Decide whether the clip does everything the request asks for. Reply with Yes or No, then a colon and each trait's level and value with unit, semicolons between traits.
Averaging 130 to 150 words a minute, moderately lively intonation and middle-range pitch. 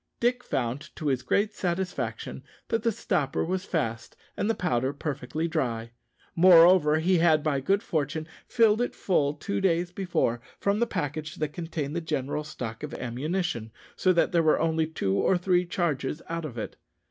No: average, 175 wpm; average, 4.5 semitones; medium, 160 Hz